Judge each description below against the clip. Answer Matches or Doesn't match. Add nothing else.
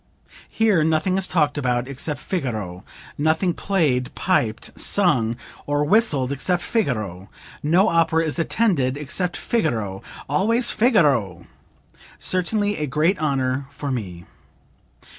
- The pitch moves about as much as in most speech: Doesn't match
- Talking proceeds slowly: Matches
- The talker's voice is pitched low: Doesn't match